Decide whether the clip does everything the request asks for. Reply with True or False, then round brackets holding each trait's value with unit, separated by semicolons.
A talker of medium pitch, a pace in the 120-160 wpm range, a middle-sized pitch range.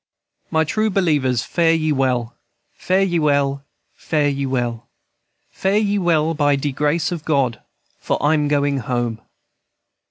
True (145 Hz; 140 wpm; 3.5 semitones)